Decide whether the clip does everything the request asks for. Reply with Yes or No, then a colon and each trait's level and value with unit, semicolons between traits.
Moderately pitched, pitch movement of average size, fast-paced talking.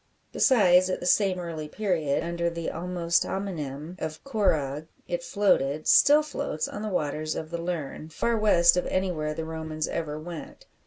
No: medium, 170 Hz; average, 3.0 semitones; average, 165 wpm